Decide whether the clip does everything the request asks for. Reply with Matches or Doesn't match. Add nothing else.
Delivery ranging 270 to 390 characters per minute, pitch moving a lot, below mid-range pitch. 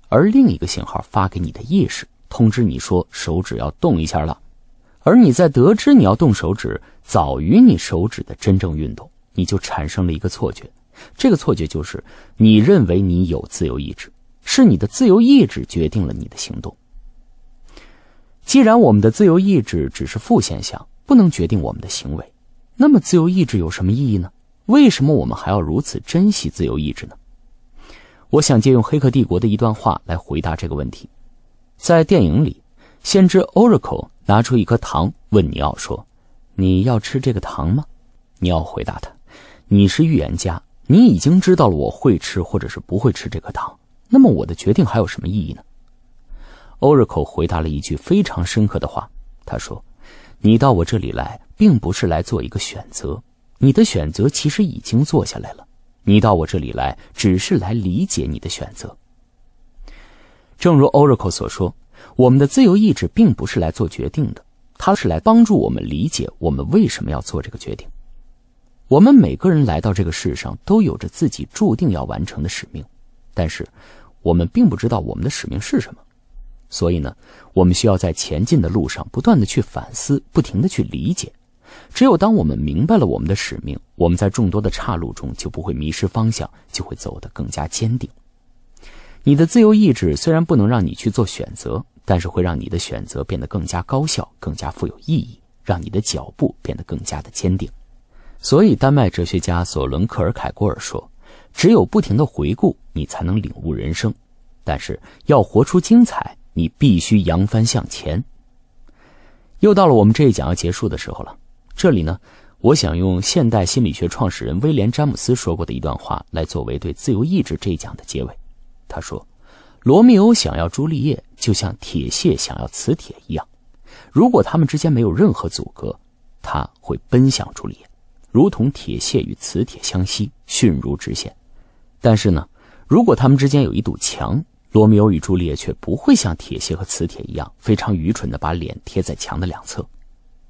Matches